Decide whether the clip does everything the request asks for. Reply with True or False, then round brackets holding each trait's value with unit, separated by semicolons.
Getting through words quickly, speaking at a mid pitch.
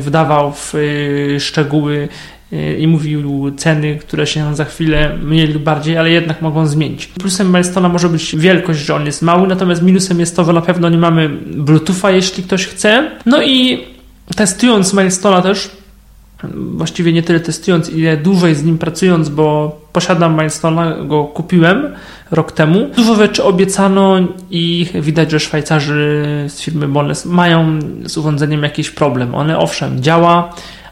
False (150 wpm; 165 Hz)